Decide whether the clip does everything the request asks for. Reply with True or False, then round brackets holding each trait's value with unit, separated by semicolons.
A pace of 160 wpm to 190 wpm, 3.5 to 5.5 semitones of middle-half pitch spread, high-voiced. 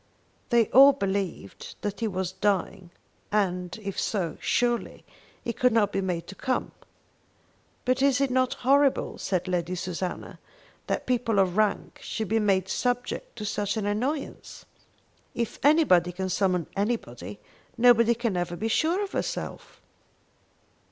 False (145 wpm; 4.8 semitones; 205 Hz)